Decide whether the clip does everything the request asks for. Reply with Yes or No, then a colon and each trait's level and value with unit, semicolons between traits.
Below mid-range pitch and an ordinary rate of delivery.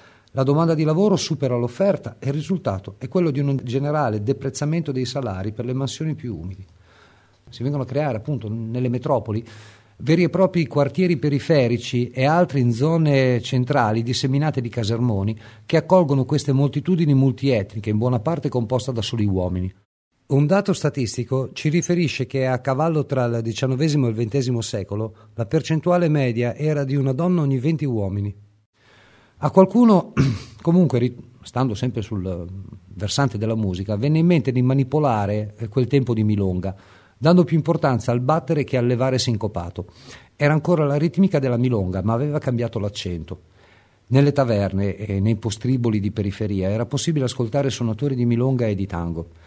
Yes: low, 125 Hz; average, 160 wpm